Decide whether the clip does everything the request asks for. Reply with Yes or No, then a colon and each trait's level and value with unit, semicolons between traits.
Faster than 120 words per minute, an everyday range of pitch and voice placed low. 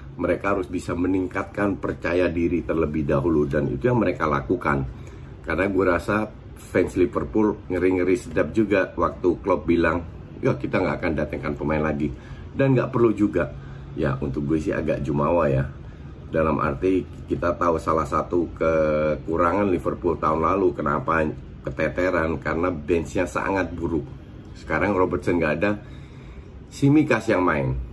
Yes: fast, 140 wpm; average, 4.4 semitones; very low, 85 Hz